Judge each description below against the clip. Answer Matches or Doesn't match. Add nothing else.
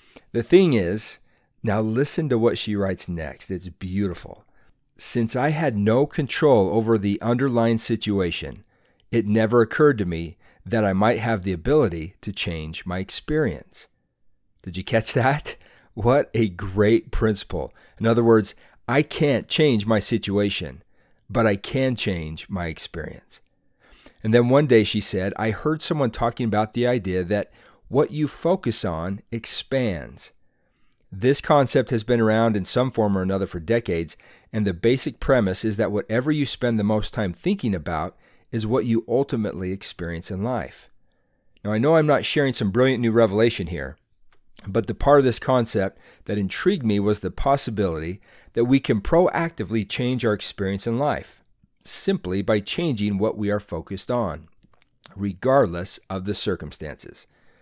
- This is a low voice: Matches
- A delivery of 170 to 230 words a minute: Doesn't match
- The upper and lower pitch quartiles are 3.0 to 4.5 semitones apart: Matches